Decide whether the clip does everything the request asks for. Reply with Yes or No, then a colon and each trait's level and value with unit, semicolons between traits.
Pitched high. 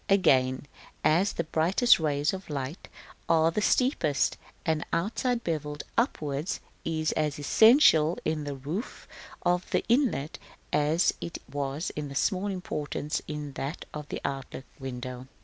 No: medium, 155 Hz